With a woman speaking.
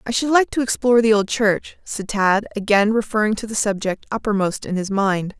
Yes: female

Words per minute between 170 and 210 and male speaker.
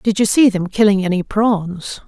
No: average, 200 wpm; female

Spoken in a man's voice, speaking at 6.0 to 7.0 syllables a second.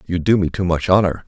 Yes: male; 6.2 syllables/s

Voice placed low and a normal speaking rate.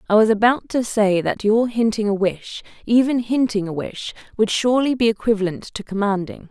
No: high, 215 Hz; average, 185 wpm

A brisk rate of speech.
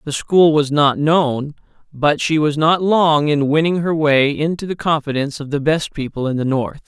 Yes: fast, 210 wpm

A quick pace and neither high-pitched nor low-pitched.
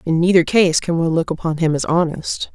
Yes: fast, 235 wpm; medium, 165 Hz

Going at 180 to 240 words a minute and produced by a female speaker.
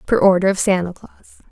Yes: average, 200 wpm; female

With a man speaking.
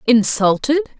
No: female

